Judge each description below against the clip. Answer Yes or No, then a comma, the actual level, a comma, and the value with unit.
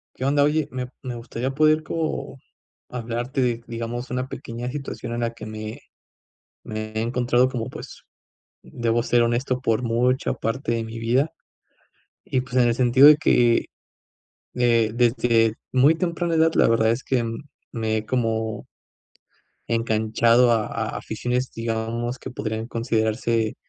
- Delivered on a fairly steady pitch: Yes, narrow, 2.0 semitones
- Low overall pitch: Yes, low, 120 Hz